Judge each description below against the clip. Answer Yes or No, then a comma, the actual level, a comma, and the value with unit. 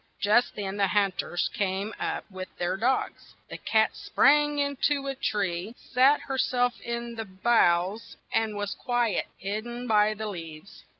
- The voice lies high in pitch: Yes, high, 215 Hz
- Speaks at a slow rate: No, average, 170 wpm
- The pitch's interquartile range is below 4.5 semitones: Yes, average, 4.0 semitones